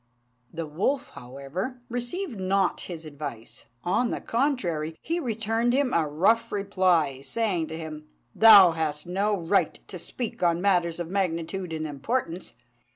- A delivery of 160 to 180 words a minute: No, average, 145 wpm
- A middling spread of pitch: No, wide, 5.9 semitones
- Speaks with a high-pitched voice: No, medium, 180 Hz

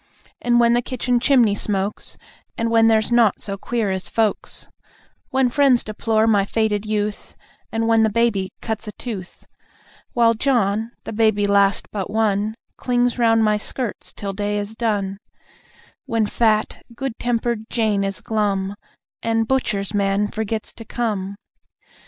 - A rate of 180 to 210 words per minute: No, average, 150 wpm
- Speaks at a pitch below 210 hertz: No, high, 220 Hz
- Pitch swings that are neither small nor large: No, narrow, 2.3 semitones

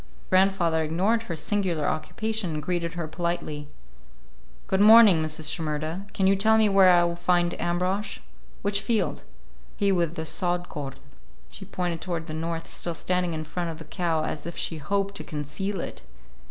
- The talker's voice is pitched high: No, medium, 175 Hz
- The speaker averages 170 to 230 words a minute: Yes, average, 175 wpm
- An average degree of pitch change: Yes, average, 3.3 semitones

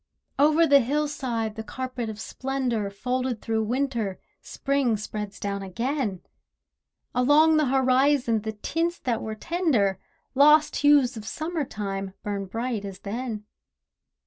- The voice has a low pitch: No, high, 245 Hz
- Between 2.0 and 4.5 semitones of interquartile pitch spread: No, average, 4.9 semitones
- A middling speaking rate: No, slow, 130 wpm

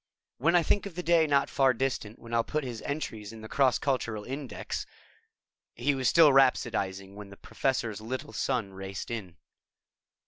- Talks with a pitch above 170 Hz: No, low, 125 Hz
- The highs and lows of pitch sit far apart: No, average, 4.6 semitones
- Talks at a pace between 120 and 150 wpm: No, average, 180 wpm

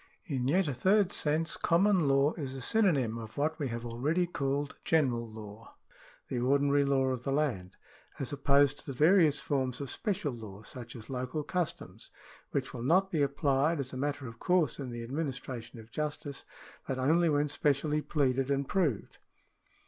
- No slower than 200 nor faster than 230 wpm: No, average, 180 wpm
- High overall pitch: No, medium, 140 Hz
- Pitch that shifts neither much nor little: Yes, average, 3.3 semitones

